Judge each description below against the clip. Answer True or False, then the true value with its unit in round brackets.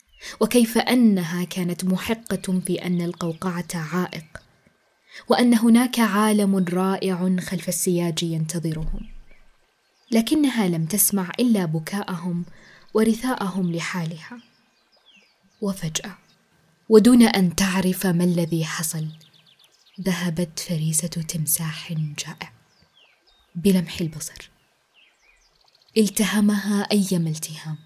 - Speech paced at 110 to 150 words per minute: False (80 wpm)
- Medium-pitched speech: True (180 Hz)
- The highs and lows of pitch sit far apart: False (3.5 semitones)